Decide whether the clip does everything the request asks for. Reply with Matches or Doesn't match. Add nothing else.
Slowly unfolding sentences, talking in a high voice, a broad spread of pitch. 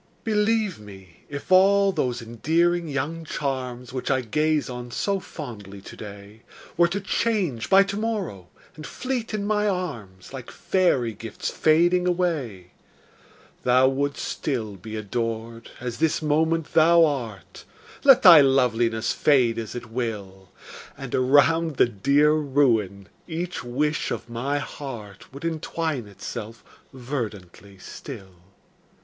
Doesn't match